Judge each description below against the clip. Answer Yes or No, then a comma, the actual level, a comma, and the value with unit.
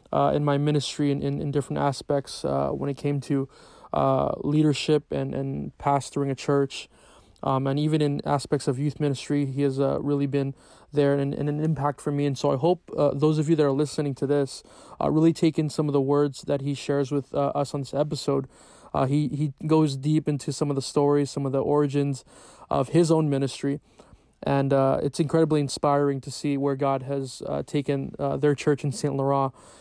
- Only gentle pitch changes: Yes, narrow, 1.2 semitones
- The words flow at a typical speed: No, fast, 215 wpm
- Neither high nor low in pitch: Yes, medium, 145 Hz